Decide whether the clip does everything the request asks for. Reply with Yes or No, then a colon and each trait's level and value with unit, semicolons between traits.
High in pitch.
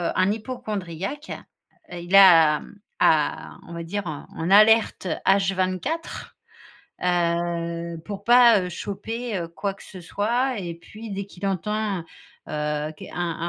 Yes: high, 195 Hz